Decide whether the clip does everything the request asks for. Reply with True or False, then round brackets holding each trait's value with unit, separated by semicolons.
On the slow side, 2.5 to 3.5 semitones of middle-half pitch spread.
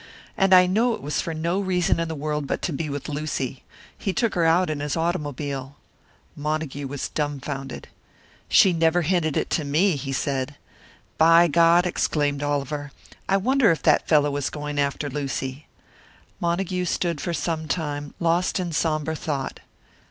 False (165 wpm; 3.1 semitones)